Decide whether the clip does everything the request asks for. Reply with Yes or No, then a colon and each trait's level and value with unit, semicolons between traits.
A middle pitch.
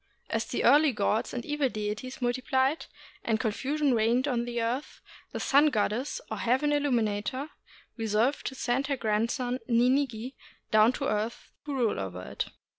No: high, 245 Hz